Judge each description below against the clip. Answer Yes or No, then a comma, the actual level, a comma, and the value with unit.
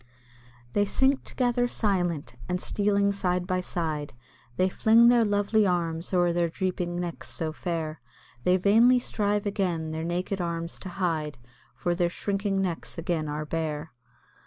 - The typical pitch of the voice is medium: Yes, medium, 180 Hz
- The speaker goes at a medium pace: Yes, average, 150 wpm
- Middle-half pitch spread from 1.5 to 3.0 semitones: No, average, 3.4 semitones